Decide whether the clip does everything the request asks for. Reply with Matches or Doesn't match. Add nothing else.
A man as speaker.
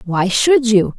Doesn't match